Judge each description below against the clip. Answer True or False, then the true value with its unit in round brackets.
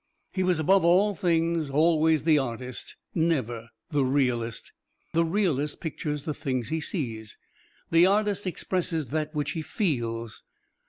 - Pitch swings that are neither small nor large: True (4.6 semitones)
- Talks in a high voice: False (155 Hz)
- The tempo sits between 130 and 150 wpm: True (140 wpm)